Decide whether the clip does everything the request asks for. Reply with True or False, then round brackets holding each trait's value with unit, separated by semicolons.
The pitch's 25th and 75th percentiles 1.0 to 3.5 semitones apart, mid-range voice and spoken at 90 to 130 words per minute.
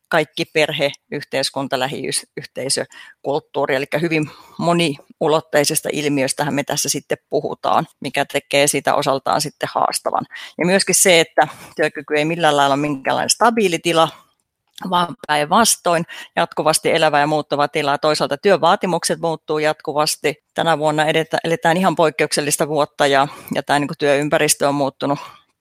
True (2.4 semitones; 155 Hz; 125 wpm)